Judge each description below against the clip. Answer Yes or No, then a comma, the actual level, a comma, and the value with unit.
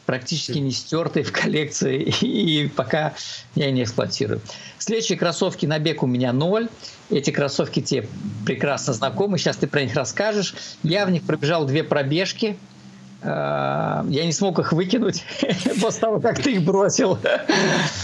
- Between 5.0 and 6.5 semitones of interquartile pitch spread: Yes, wide, 5.4 semitones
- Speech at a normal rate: Yes, average, 145 wpm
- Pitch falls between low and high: Yes, medium, 165 Hz